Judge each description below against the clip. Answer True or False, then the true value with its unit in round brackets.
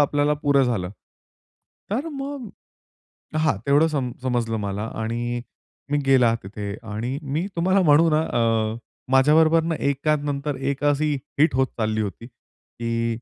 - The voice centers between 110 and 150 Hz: True (140 Hz)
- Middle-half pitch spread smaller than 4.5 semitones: False (4.8 semitones)